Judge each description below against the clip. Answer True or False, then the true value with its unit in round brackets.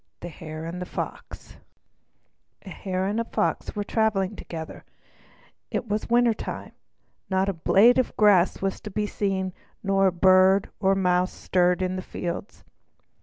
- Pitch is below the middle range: False (190 Hz)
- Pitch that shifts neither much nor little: False (2.3 semitones)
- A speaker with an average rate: True (160 wpm)